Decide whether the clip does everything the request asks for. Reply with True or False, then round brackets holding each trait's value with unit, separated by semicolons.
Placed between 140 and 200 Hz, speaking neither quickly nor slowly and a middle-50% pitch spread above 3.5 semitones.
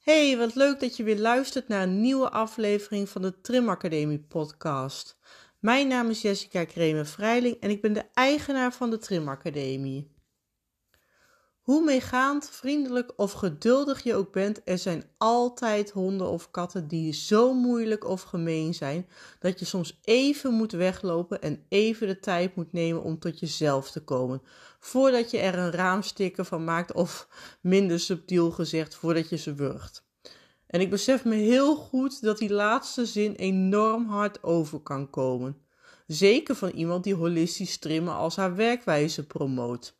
True (190 Hz; 160 wpm; 5.6 semitones)